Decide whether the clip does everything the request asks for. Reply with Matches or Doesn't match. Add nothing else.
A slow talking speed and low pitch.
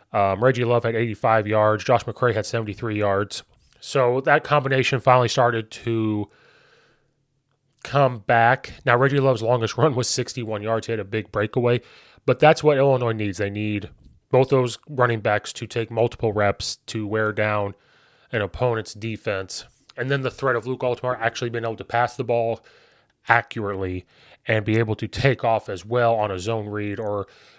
Doesn't match